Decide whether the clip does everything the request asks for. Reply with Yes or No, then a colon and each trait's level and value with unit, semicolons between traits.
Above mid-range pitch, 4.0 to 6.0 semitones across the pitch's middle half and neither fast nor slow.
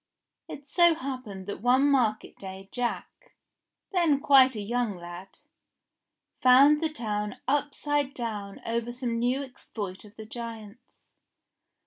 No: high, 240 Hz; average, 4.8 semitones; slow, 130 wpm